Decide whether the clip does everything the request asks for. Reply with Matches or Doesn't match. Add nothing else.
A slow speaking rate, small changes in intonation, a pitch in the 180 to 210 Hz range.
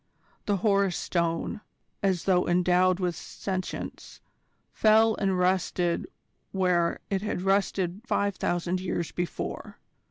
Matches